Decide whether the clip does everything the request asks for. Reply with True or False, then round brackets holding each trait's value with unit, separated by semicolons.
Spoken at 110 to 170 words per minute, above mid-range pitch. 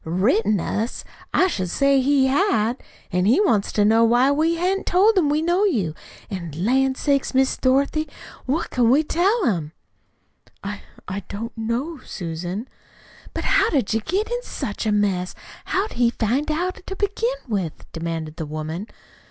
True (165 wpm; 245 Hz)